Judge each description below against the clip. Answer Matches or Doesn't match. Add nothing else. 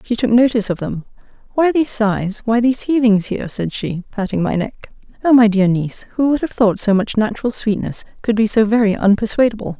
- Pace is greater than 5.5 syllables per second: Matches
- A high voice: Matches